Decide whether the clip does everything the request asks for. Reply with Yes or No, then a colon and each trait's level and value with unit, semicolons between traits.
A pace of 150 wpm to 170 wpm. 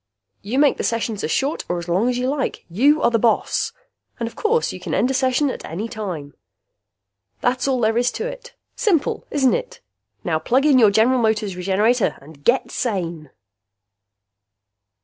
No: average, 185 wpm